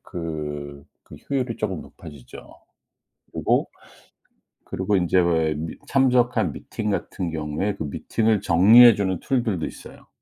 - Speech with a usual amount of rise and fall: No, wide, 5.8 semitones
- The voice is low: Yes, very low, 95 Hz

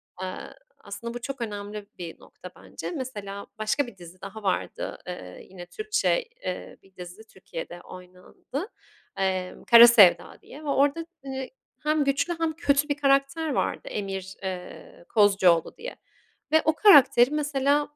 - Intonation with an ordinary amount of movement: No, wide, 7.2 semitones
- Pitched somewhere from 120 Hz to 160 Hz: No, high, 235 Hz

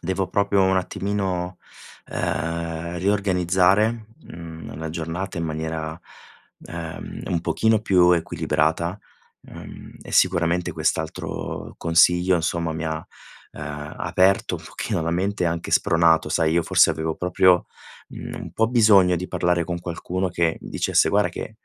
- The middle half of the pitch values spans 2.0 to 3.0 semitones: Yes, narrow, 2.4 semitones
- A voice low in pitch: Yes, very low, 85 Hz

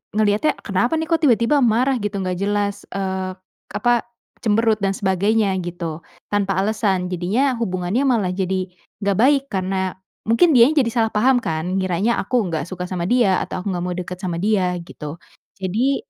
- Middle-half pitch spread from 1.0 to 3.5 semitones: No, average, 3.9 semitones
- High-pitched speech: Yes, high, 200 Hz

